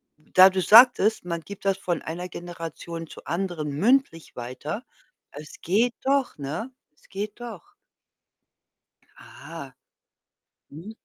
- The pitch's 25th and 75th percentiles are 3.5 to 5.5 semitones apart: Yes, average, 4.6 semitones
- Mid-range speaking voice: Yes, medium, 180 Hz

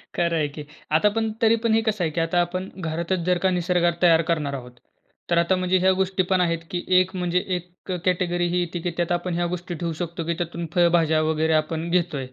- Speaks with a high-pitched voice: No, medium, 175 Hz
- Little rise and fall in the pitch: Yes, narrow, 1.7 semitones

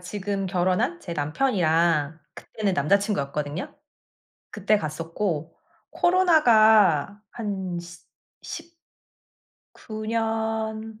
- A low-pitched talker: No, high, 200 Hz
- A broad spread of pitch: No, average, 4.7 semitones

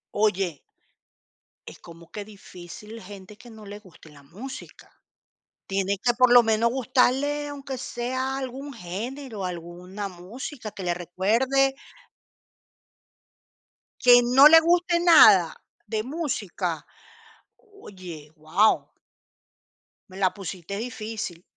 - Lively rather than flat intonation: Yes, wide, 6.0 semitones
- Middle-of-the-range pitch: No, high, 215 Hz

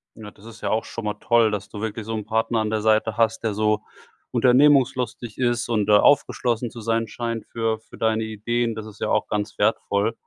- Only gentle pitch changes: Yes, narrow, 1.6 semitones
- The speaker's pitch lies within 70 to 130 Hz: Yes, low, 110 Hz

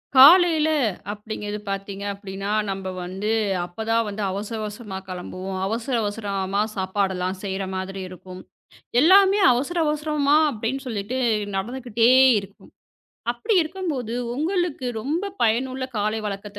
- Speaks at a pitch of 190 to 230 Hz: Yes, high, 215 Hz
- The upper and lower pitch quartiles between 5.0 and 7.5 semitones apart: Yes, average, 5.3 semitones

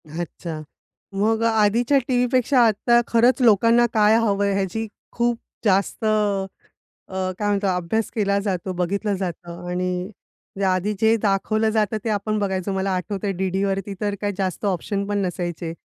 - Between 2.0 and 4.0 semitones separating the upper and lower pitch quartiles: Yes, average, 2.7 semitones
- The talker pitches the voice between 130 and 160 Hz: No, high, 200 Hz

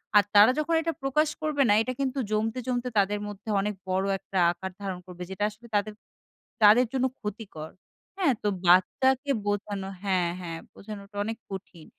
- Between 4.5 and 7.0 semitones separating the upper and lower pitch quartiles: Yes, average, 4.8 semitones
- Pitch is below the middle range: No, high, 210 Hz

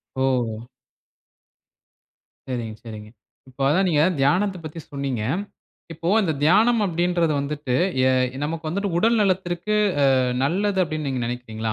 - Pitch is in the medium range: Yes, medium, 155 Hz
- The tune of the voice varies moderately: No, wide, 6.0 semitones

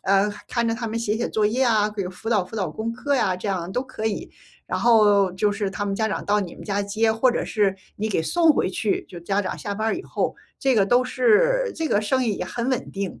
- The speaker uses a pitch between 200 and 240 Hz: Yes, high, 215 Hz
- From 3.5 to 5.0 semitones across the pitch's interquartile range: No, average, 3.0 semitones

